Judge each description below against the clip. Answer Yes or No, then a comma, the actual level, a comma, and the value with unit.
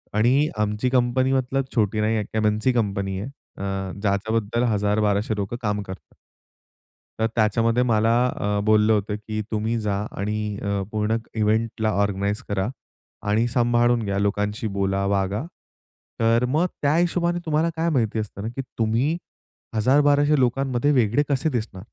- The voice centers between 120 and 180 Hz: No, low, 110 Hz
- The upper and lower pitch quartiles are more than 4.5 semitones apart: No, average, 3.2 semitones